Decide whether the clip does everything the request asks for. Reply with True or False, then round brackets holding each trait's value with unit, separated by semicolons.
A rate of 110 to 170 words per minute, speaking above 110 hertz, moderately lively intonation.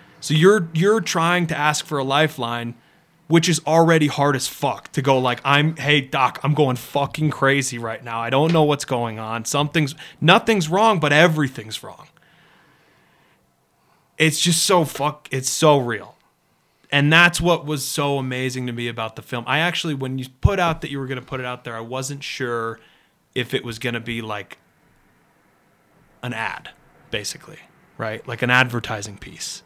False (180 wpm; 140 Hz; 4.2 semitones)